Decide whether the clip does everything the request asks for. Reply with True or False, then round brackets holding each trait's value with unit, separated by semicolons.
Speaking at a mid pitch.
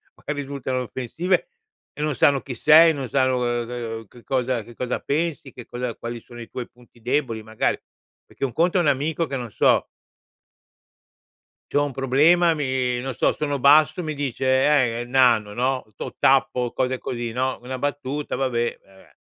False (130 Hz)